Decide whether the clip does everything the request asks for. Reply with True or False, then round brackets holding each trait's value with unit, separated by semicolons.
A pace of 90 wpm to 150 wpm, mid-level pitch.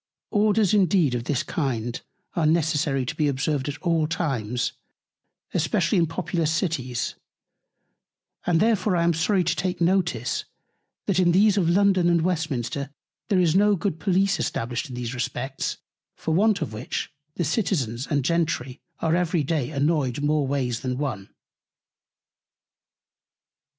True (145 wpm; 160 Hz)